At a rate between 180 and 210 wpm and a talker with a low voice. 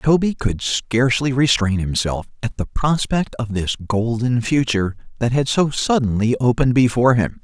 No: average, 155 wpm; low, 120 Hz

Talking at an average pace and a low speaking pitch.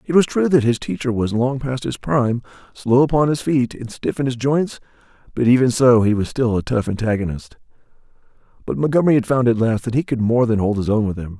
No: fast, 235 wpm; low, 120 Hz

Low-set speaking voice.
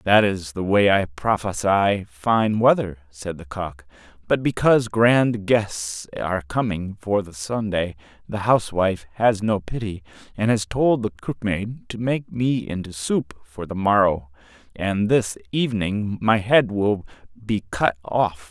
Yes: low, 100 Hz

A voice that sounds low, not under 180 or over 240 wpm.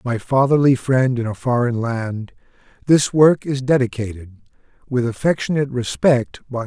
No: low, 125 Hz; slow, 135 wpm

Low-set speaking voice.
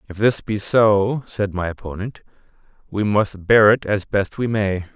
Yes: low, 105 Hz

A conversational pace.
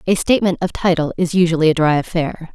No: fast, 210 wpm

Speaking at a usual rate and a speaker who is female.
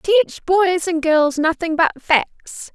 Yes: average, 155 wpm; female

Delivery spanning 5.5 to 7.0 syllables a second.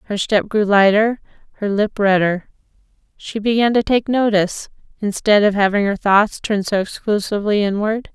No: 5.2 syllables/s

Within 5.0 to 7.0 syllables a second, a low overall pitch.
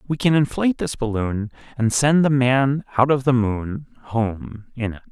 No: 4.5 syllables/s; low, 125 Hz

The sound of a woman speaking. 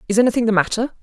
Yes: female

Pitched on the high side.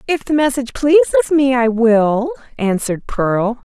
Yes: very high, 250 Hz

